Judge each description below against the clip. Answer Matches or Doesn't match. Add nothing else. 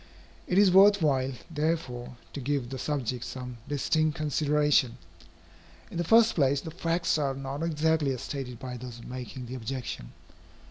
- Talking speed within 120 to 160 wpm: Matches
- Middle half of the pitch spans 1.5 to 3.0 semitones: Doesn't match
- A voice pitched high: Doesn't match